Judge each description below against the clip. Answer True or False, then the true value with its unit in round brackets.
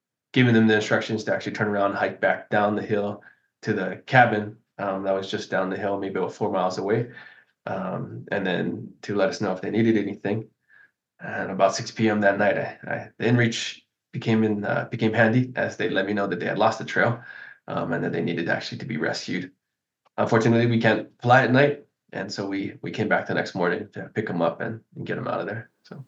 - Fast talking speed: True (235 wpm)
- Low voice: True (110 Hz)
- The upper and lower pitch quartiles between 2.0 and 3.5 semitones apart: True (2.6 semitones)